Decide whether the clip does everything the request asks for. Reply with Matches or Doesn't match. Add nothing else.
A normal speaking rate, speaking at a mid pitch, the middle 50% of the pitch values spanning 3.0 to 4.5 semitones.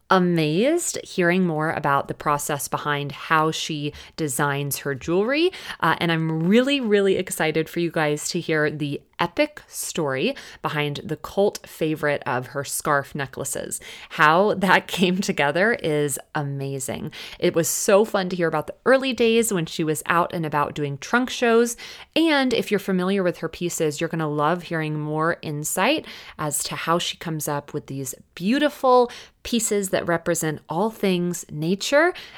Doesn't match